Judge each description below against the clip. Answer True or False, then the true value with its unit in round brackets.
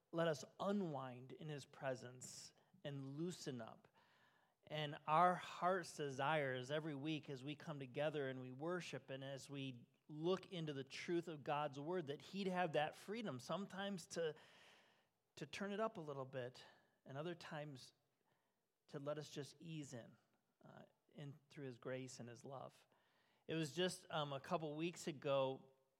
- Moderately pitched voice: True (150 Hz)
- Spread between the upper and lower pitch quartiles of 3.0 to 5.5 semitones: True (4.0 semitones)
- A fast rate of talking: False (165 wpm)